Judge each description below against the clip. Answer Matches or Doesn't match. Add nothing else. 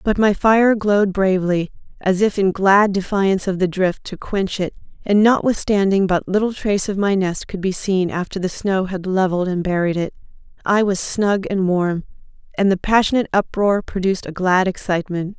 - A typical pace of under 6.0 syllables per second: Matches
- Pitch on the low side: Doesn't match